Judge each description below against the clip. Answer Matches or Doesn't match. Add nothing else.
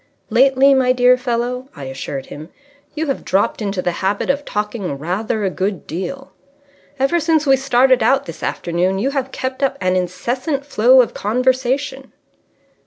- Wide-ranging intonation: Matches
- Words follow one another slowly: Doesn't match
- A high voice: Matches